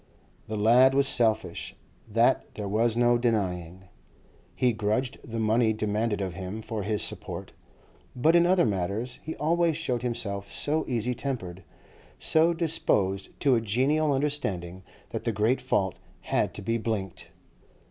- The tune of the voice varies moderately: Yes, average, 4.5 semitones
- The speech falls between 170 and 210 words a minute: No, average, 145 wpm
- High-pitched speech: No, low, 115 Hz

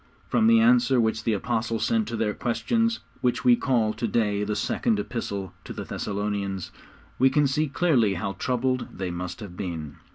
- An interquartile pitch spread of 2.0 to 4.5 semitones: No, average, 5.2 semitones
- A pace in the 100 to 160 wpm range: No, average, 185 wpm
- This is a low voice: Yes, low, 115 Hz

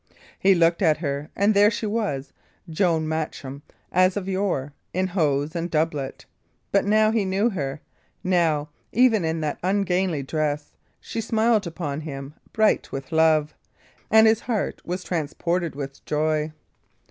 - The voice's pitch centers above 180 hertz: No, medium, 170 Hz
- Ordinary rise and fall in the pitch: Yes, average, 4.8 semitones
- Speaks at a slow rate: No, average, 145 wpm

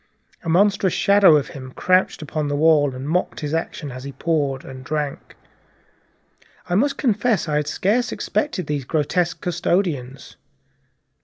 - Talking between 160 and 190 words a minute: No, average, 150 wpm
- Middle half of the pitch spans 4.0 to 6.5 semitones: Yes, average, 4.3 semitones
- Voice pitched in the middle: Yes, medium, 160 Hz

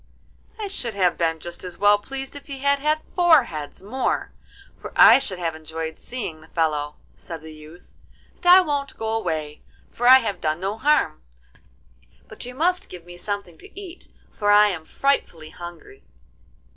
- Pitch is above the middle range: Yes, high, 205 Hz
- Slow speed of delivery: No, average, 180 wpm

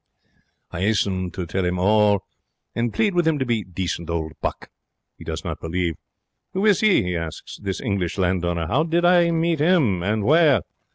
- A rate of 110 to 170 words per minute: No, average, 185 wpm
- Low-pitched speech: Yes, low, 100 Hz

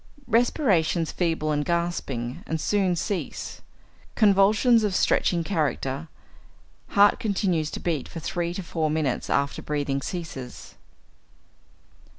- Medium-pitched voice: Yes, medium, 170 Hz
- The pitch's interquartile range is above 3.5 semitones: Yes, average, 4.5 semitones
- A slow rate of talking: Yes, slow, 115 wpm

